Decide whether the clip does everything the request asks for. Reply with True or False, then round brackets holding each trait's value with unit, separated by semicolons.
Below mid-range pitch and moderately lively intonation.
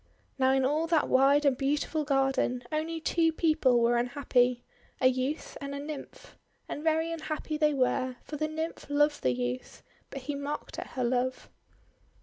False (280 Hz; 3.1 semitones)